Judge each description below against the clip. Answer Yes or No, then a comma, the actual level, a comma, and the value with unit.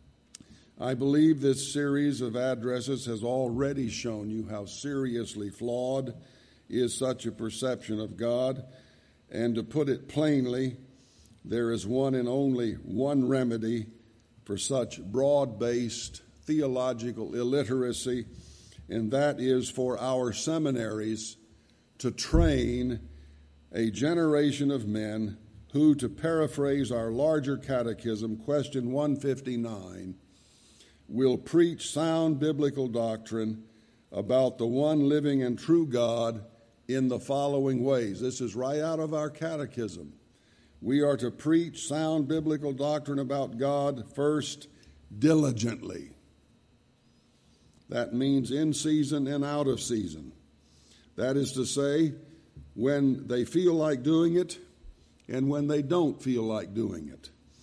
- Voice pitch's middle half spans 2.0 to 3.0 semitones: No, average, 3.9 semitones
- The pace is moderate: No, slow, 120 wpm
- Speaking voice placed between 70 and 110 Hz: No, low, 130 Hz